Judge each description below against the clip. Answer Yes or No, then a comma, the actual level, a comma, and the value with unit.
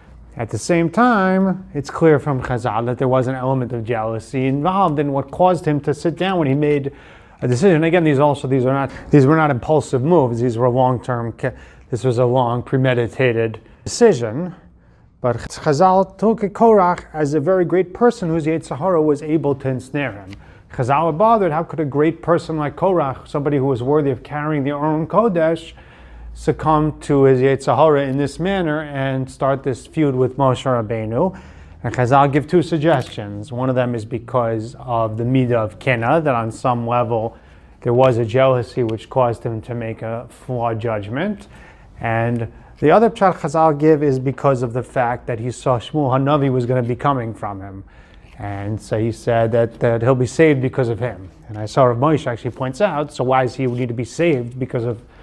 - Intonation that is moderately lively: Yes, average, 4.5 semitones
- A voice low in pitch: Yes, low, 130 Hz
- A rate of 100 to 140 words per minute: No, average, 195 wpm